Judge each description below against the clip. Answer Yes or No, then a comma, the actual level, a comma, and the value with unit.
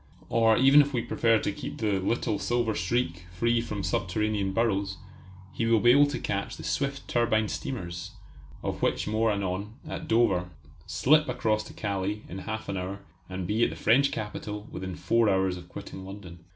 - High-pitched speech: No, low, 105 Hz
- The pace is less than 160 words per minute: No, average, 185 wpm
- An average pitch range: Yes, average, 3.4 semitones